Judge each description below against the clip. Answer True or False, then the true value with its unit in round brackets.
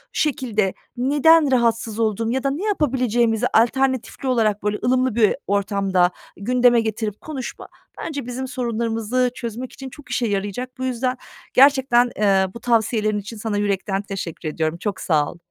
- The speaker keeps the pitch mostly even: False (3.7 semitones)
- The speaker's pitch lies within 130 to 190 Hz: False (235 Hz)